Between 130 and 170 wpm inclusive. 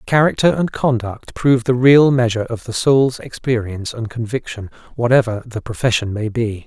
Yes: average, 160 wpm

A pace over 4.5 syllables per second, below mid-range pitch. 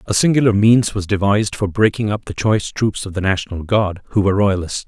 Yes: 6.0 syllables/s; low, 100 Hz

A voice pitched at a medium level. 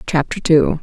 Yes: medium, 160 Hz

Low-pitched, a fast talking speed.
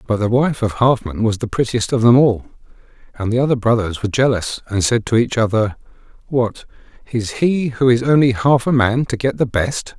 Yes: low, 120 Hz; fast, 210 wpm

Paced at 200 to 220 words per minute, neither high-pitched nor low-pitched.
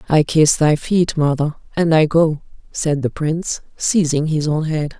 No: average, 180 wpm; medium, 155 Hz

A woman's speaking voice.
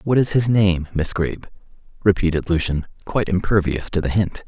No: male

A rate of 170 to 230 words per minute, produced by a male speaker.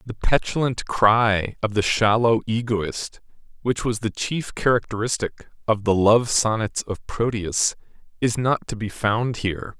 No: average, 145 wpm; male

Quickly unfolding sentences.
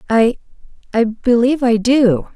No: slow, 100 wpm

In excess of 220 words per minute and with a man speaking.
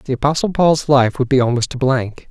Yes: fast, 235 wpm; male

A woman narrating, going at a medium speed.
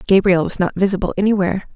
Yes: female; average, 170 wpm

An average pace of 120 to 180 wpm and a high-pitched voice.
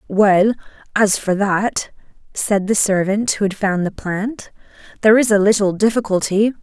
Yes: average, 155 wpm; high, 205 Hz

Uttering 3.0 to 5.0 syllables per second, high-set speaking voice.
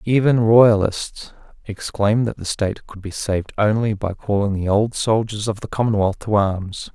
No: 4.8 syllables/s; low, 105 Hz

